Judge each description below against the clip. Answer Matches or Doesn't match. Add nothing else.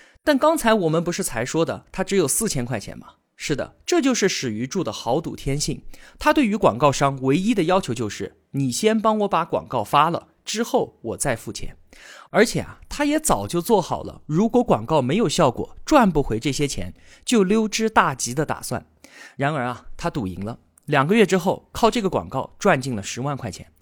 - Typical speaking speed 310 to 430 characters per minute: Doesn't match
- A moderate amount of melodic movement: Doesn't match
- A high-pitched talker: Doesn't match